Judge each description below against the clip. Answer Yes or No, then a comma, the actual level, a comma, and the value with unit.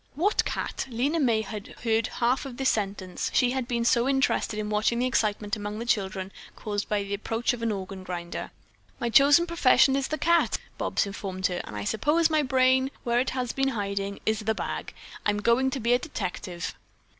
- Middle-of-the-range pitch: No, high, 230 Hz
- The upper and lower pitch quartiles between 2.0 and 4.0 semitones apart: No, average, 4.4 semitones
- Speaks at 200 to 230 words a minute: Yes, fast, 205 wpm